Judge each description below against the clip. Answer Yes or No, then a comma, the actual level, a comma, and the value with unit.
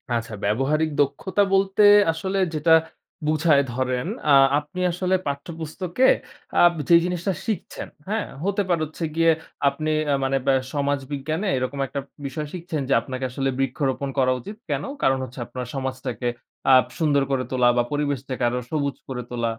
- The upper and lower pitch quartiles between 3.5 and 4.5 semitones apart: Yes, average, 4.2 semitones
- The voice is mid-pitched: Yes, medium, 145 Hz